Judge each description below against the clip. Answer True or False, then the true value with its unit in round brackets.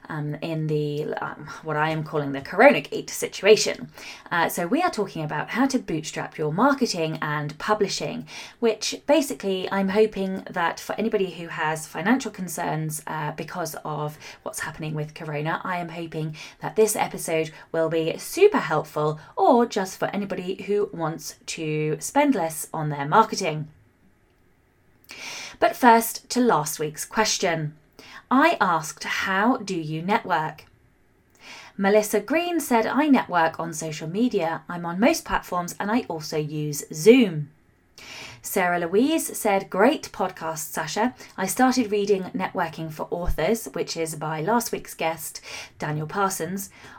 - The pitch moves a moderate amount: False (5.9 semitones)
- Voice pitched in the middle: True (170 Hz)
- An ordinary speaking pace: True (145 wpm)